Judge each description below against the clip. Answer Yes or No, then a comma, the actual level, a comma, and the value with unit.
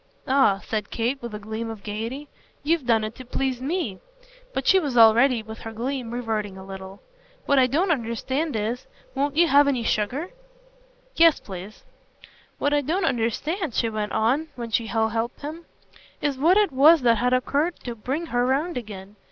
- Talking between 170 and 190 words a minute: Yes, average, 185 wpm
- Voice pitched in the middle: No, high, 245 Hz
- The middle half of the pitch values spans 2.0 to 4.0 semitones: No, average, 4.6 semitones